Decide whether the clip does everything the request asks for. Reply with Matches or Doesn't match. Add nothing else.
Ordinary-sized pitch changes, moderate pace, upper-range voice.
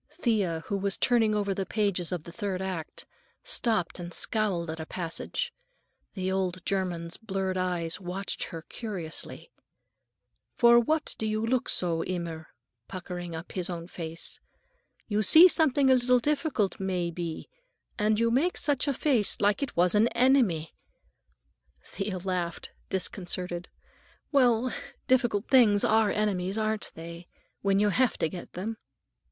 Matches